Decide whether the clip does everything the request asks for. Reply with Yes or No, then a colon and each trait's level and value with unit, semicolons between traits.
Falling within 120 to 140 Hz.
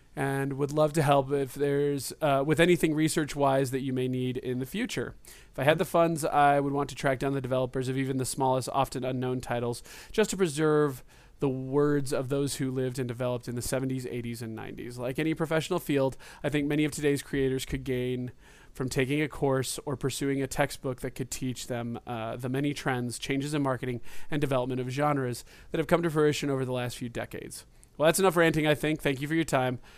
Yes: low, 135 Hz